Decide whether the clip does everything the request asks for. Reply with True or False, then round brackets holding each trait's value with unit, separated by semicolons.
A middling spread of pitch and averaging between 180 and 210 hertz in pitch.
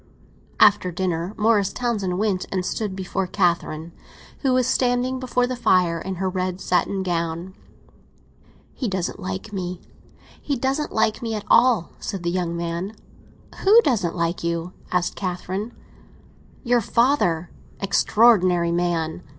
True (4.6 semitones; 190 Hz)